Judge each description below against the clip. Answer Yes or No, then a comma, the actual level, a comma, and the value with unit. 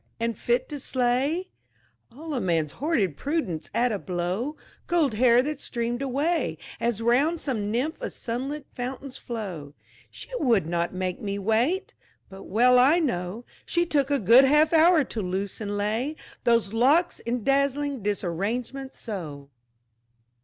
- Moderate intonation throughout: No, wide, 5.8 semitones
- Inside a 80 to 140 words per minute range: No, average, 150 wpm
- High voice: Yes, high, 240 Hz